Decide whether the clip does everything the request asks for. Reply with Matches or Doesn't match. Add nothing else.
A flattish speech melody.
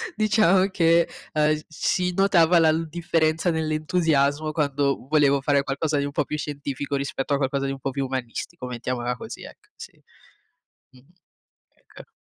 Doesn't match